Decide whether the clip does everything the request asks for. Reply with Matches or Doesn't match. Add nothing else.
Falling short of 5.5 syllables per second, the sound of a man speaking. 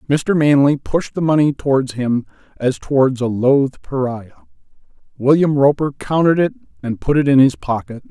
Matches